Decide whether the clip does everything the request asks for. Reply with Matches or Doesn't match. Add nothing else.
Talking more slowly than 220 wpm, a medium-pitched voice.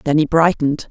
Matches